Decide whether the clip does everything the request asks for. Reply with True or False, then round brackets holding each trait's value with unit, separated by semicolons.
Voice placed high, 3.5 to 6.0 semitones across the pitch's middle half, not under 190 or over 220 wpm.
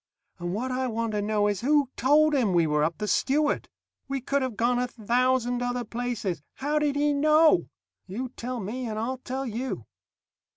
True (245 Hz; 3.8 semitones; 195 wpm)